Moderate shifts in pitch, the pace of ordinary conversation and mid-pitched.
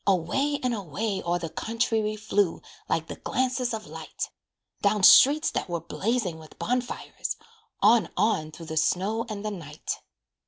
No: average, 5.0 semitones; average, 160 wpm; high, 210 Hz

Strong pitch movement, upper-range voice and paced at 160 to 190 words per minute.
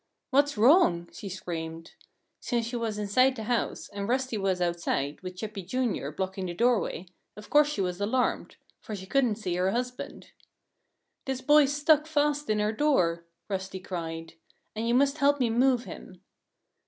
Yes: wide, 5.9 semitones; high, 215 Hz; average, 165 wpm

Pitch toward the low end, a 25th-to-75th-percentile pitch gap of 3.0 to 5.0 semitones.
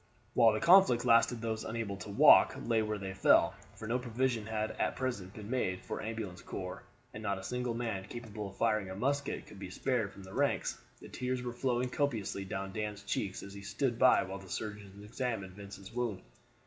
Yes: low, 110 Hz; average, 3.5 semitones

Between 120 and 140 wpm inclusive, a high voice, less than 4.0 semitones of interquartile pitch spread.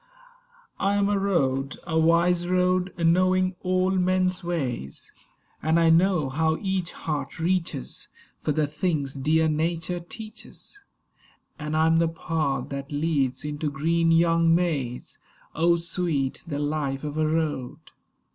No: slow, 135 wpm; medium, 165 Hz; average, 3.3 semitones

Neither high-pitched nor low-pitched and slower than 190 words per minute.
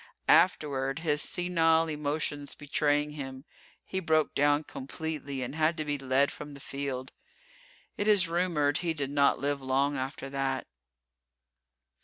Yes: medium, 145 Hz; average, 140 wpm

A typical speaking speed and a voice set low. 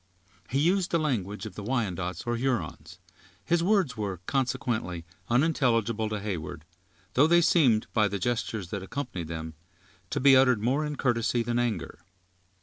Yes: average, 155 wpm; low, 120 Hz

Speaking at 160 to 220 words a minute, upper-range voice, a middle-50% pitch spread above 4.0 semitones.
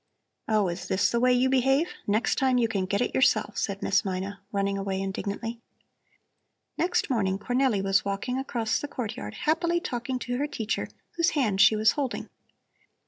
Yes: average, 175 wpm; high, 230 Hz; average, 4.8 semitones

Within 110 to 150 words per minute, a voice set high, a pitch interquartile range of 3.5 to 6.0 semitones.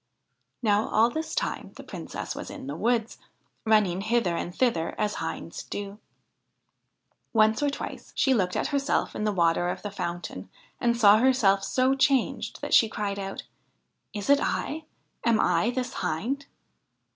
No: average, 165 wpm; high, 215 Hz; average, 4.7 semitones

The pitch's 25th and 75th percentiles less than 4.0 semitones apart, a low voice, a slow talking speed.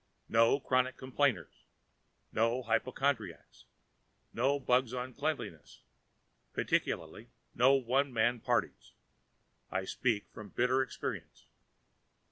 Yes: average, 2.7 semitones; low, 125 Hz; slow, 95 wpm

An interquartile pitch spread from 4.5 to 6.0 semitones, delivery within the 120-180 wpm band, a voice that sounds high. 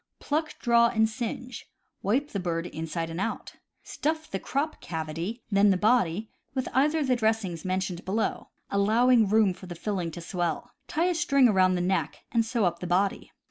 No: wide, 5.4 semitones; average, 190 wpm; high, 210 Hz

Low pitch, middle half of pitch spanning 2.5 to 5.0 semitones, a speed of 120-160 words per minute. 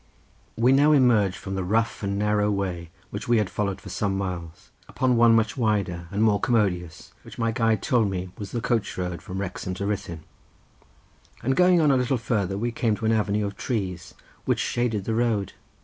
No: low, 105 Hz; average, 3.2 semitones; average, 200 wpm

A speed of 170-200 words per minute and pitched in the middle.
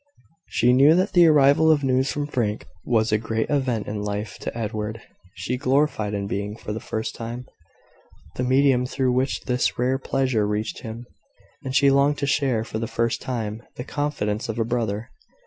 No: average, 185 wpm; low, 125 Hz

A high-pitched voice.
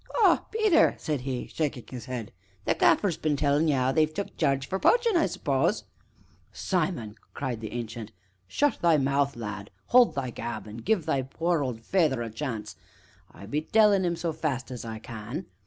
No: medium, 140 Hz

